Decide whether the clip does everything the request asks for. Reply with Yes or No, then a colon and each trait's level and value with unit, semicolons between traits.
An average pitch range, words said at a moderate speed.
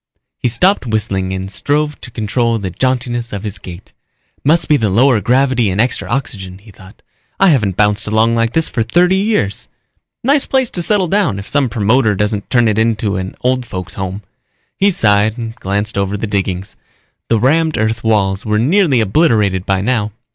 Yes: average, 4.7 semitones; average, 185 wpm